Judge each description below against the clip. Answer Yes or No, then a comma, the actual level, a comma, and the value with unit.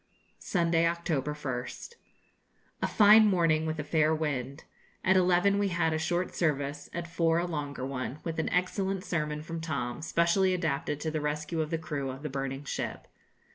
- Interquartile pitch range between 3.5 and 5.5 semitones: No, average, 2.8 semitones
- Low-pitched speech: No, medium, 160 Hz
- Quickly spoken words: No, average, 175 wpm